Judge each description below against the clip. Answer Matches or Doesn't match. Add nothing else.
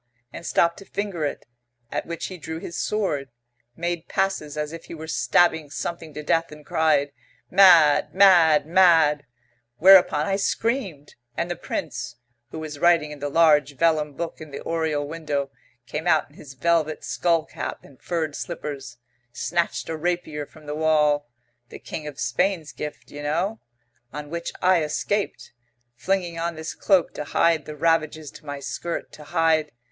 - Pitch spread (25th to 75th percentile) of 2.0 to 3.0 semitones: Matches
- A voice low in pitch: Doesn't match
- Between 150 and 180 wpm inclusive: Matches